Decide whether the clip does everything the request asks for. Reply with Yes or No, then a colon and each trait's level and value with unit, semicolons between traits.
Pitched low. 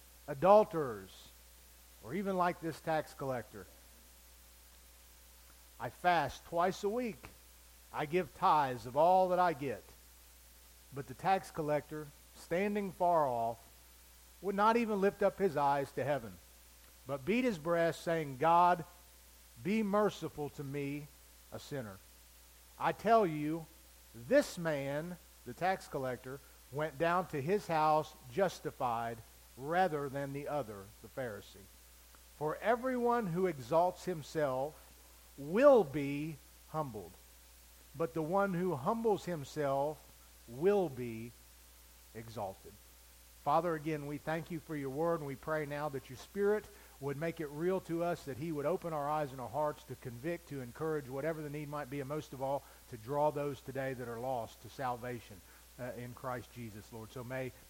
No: medium, 145 Hz